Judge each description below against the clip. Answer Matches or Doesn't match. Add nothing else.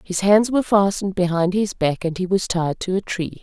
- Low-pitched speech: Doesn't match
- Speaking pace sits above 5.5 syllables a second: Doesn't match